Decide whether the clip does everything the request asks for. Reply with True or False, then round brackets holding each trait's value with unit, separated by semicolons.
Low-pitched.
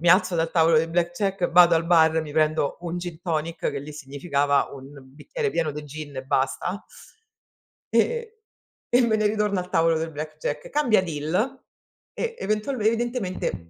False (170 Hz)